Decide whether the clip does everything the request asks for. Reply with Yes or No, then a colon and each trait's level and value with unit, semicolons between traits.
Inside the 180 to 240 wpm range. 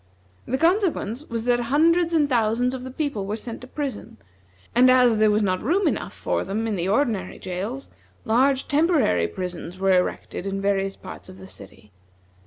Yes: average, 185 wpm